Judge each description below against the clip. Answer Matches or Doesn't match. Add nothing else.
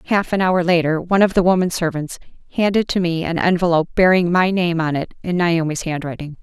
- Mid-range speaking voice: Matches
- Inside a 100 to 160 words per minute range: Doesn't match